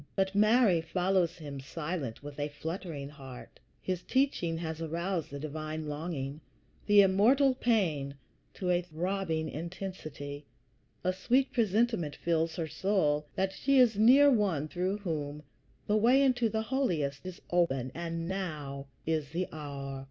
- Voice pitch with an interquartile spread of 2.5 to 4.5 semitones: No, average, 5.0 semitones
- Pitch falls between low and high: Yes, medium, 170 Hz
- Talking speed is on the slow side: No, average, 145 wpm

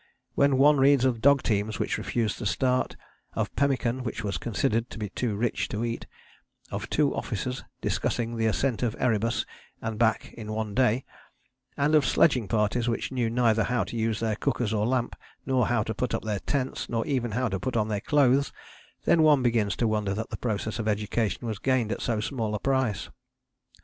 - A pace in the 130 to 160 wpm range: No, average, 200 wpm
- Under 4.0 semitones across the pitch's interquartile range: Yes, average, 3.0 semitones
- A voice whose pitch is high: No, low, 115 Hz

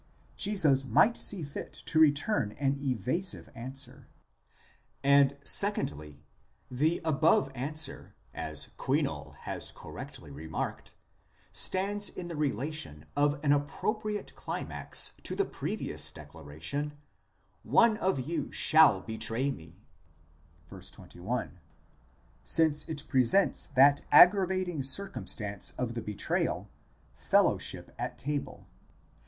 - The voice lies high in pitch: No, medium, 140 Hz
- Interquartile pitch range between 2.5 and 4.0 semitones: No, average, 5.2 semitones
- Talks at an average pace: No, slow, 105 wpm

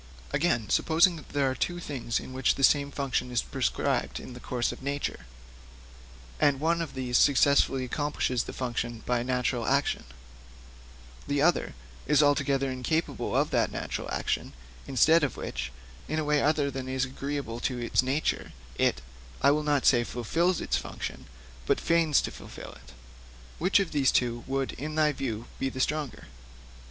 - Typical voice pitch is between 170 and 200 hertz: No, low, 135 Hz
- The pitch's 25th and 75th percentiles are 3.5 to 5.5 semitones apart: No, average, 3.0 semitones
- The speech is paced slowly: No, average, 165 wpm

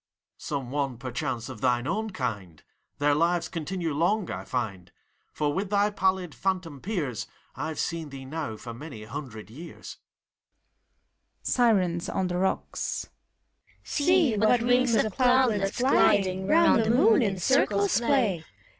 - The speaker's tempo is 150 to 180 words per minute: No, slow, 135 wpm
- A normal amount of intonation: No, wide, 7.8 semitones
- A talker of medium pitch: Yes, medium, 175 Hz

